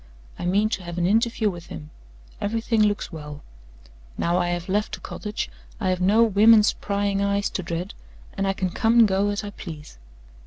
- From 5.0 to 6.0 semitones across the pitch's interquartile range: No, average, 3.2 semitones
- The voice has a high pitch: Yes, high, 200 Hz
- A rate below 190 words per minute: No, average, 195 wpm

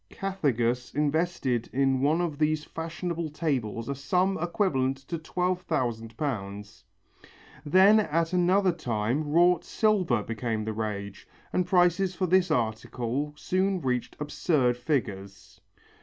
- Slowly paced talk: Yes, slow, 125 wpm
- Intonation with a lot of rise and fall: Yes, wide, 6.9 semitones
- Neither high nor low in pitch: Yes, medium, 150 Hz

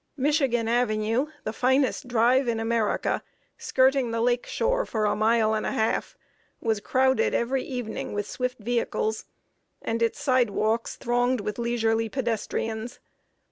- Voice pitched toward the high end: Yes, high, 235 Hz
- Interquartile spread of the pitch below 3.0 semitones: Yes, narrow, 2.4 semitones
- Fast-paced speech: No, average, 140 wpm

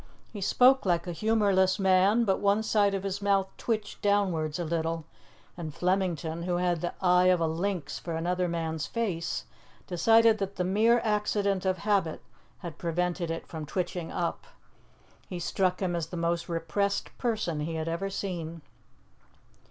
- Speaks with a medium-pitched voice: Yes, medium, 180 Hz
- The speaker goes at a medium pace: Yes, average, 165 wpm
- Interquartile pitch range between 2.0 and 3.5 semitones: Yes, average, 3.1 semitones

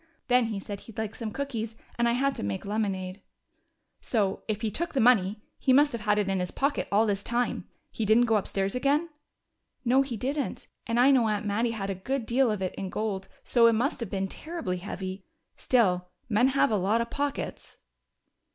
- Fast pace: Yes, fast, 210 wpm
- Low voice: No, high, 220 Hz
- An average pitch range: Yes, average, 4.0 semitones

